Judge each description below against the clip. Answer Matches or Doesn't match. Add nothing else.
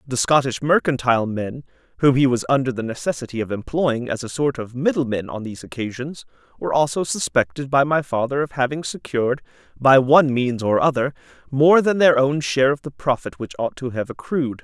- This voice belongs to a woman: Doesn't match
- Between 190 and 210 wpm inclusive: Matches